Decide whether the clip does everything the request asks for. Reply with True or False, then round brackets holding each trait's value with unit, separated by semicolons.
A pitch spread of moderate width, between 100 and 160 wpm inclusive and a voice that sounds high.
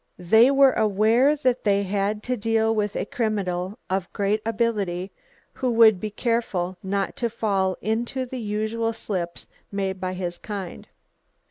True (3.1 semitones; 150 wpm; 210 Hz)